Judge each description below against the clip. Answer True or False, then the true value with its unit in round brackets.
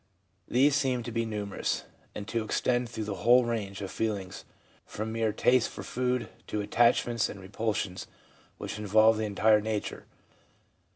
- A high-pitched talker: False (110 Hz)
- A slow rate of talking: False (155 wpm)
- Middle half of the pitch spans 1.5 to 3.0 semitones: True (2.5 semitones)